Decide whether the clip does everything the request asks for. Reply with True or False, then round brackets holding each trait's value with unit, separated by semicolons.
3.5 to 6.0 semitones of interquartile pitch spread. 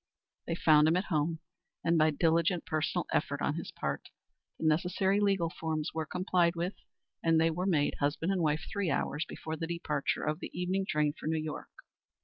False (2.4 semitones)